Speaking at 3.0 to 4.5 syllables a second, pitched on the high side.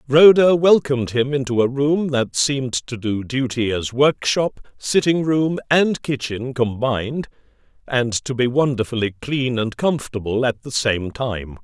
No: 4.4 syllables/s; low, 130 Hz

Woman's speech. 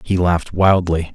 No: male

